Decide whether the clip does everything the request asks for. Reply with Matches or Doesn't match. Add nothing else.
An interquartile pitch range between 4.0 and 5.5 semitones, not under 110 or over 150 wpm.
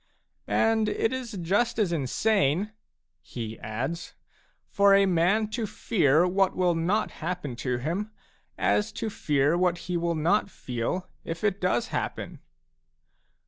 Matches